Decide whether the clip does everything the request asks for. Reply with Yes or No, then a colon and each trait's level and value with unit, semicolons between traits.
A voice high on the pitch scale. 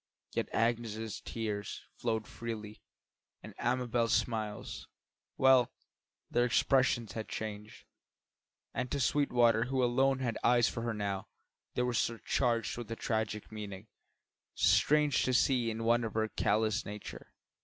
No: low, 115 Hz